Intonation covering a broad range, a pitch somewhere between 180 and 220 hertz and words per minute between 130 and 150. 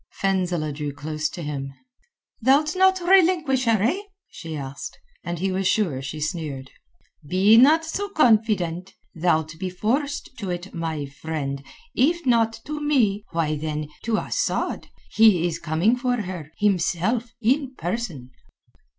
Yes: wide, 7.9 semitones; high, 190 Hz; average, 140 wpm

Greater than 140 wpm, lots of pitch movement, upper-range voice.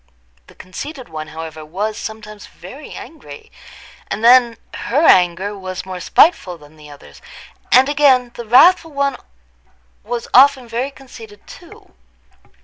No: slow, 135 wpm; wide, 6.6 semitones; high, 225 Hz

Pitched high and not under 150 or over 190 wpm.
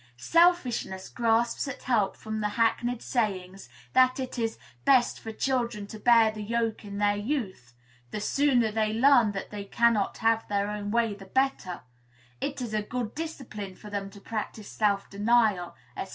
Yes: high, 220 Hz; average, 170 wpm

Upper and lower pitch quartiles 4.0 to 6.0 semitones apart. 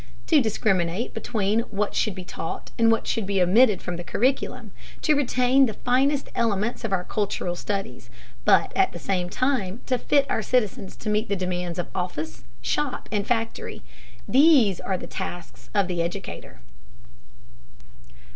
Yes: average, 5.2 semitones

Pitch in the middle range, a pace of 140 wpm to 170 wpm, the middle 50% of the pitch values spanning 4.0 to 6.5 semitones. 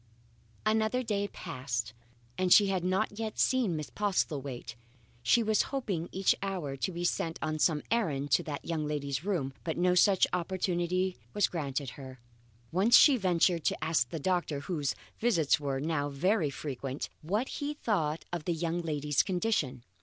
Yes: medium, 170 Hz; average, 165 wpm; average, 5.2 semitones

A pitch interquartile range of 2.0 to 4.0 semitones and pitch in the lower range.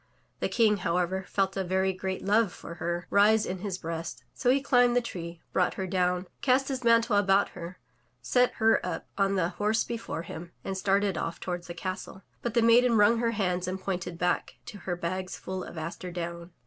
No: average, 3.7 semitones; high, 190 Hz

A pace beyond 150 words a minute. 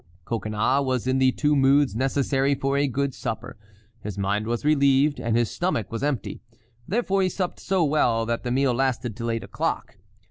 Yes: average, 180 wpm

